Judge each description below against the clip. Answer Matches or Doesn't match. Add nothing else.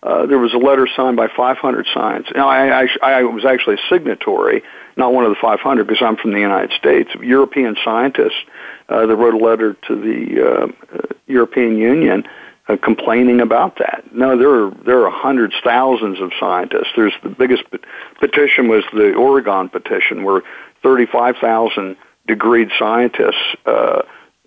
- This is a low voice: Matches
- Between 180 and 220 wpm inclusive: Doesn't match